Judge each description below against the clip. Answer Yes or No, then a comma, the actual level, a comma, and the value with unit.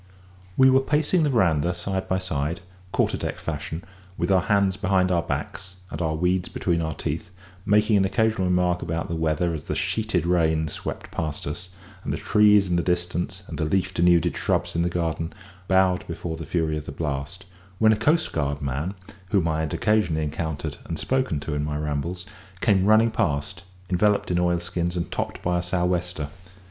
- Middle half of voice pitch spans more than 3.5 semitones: No, average, 3.2 semitones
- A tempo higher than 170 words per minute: Yes, average, 190 wpm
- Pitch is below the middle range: Yes, very low, 90 Hz